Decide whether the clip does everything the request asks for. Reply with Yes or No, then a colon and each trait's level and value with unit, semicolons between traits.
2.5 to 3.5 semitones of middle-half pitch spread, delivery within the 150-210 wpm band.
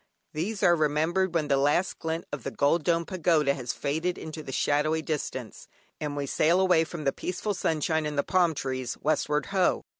Yes: average, 3.0 semitones; average, 190 wpm